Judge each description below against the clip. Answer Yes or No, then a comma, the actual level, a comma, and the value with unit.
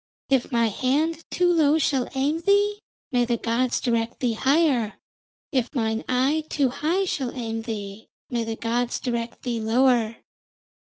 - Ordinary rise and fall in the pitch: Yes, average, 4.1 semitones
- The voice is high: Yes, very high, 250 Hz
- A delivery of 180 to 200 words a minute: No, average, 155 wpm